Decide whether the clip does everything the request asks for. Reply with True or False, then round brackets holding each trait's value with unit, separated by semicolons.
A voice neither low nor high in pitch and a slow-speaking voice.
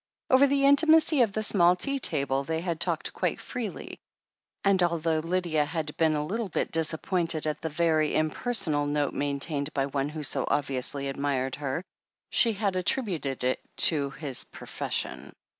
False (160 Hz; 165 wpm)